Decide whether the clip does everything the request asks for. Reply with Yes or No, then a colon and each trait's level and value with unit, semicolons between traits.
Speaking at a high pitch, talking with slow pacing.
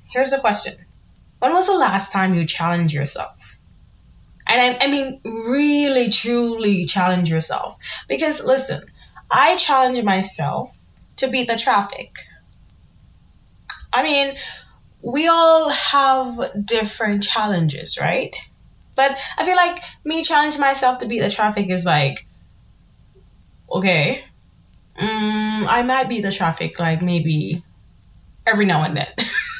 Yes: high, 215 Hz; slow, 125 wpm